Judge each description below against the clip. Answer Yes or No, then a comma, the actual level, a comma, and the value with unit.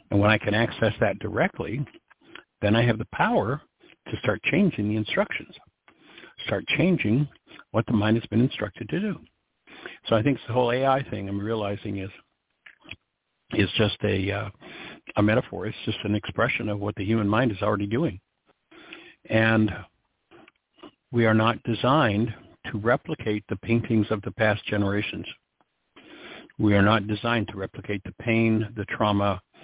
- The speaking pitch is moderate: No, low, 110 Hz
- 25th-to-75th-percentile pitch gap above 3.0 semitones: No, narrow, 2.5 semitones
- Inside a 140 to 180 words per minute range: Yes, average, 160 wpm